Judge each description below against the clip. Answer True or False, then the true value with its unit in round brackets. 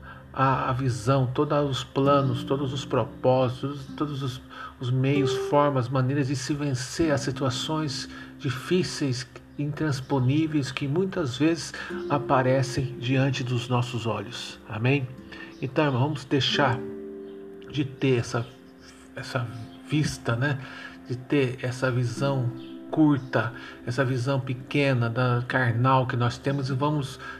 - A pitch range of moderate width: False (2.2 semitones)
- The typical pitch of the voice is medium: False (130 Hz)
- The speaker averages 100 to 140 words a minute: True (120 wpm)